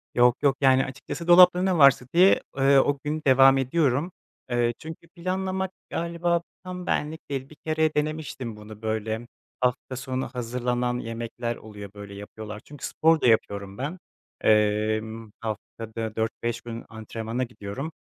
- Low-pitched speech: Yes, low, 125 Hz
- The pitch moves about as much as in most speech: No, wide, 5.7 semitones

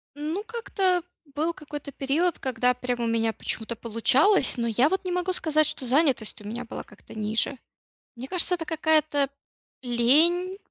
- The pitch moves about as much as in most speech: No, wide, 6.0 semitones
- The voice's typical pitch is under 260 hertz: No, very high, 285 Hz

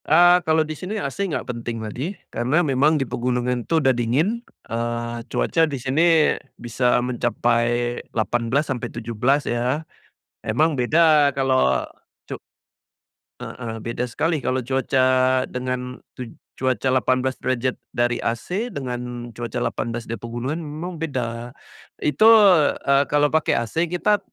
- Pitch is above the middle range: No, low, 130 Hz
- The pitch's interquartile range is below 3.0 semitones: No, average, 4.2 semitones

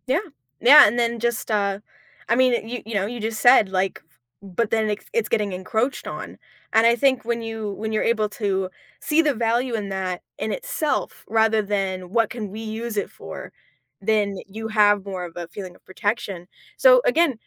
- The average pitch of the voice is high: Yes, high, 220 Hz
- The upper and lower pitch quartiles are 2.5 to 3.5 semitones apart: Yes, average, 2.9 semitones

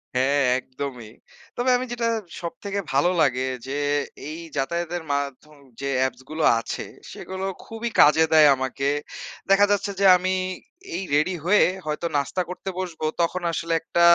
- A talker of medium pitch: Yes, medium, 160 Hz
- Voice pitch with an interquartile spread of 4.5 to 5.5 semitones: Yes, average, 5.1 semitones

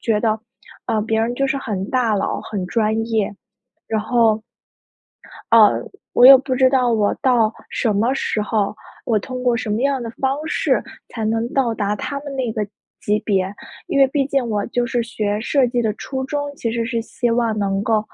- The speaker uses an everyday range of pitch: Yes, average, 3.1 semitones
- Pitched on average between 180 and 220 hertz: No, high, 230 Hz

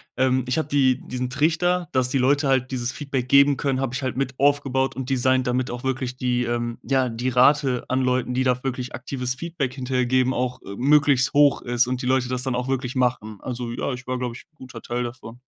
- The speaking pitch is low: Yes, low, 130 Hz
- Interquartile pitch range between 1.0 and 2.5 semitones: Yes, narrow, 1.4 semitones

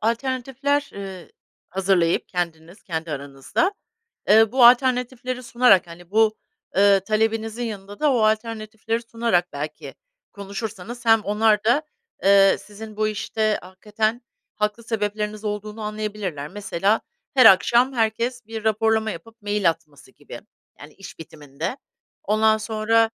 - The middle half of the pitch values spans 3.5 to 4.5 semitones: No, average, 2.7 semitones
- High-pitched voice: Yes, high, 215 Hz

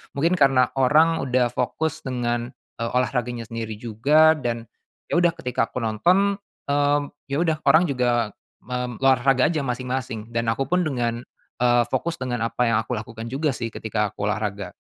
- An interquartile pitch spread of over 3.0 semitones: Yes, average, 3.7 semitones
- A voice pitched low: Yes, low, 125 Hz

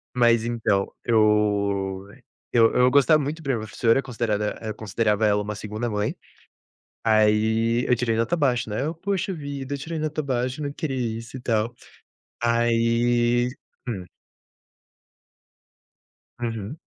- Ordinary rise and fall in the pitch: Yes, average, 3.7 semitones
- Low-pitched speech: Yes, low, 115 Hz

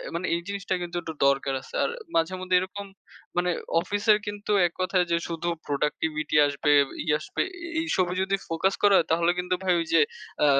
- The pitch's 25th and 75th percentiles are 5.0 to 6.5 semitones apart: No, average, 2.7 semitones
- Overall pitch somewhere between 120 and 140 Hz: No, medium, 175 Hz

